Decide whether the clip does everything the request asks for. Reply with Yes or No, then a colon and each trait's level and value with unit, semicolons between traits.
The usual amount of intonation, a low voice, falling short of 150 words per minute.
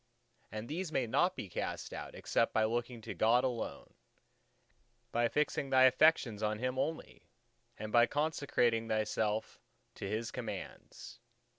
Yes: average, 3.3 semitones; low, 120 Hz; average, 140 wpm